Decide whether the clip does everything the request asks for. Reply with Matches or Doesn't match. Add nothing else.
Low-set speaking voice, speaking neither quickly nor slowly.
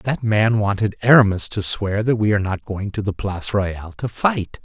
Doesn't match